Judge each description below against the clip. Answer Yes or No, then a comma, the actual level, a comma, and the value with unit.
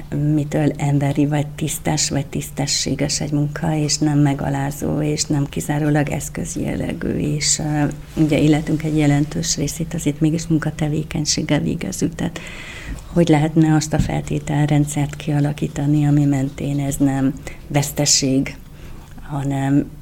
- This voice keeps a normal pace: Yes, average, 120 wpm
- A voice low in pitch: No, medium, 150 Hz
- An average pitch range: No, narrow, 1.2 semitones